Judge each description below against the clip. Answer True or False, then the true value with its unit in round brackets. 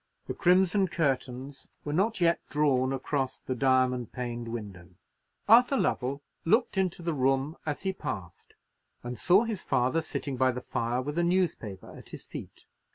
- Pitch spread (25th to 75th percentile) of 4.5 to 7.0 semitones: True (5.6 semitones)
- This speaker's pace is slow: False (160 wpm)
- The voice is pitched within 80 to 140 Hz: True (135 Hz)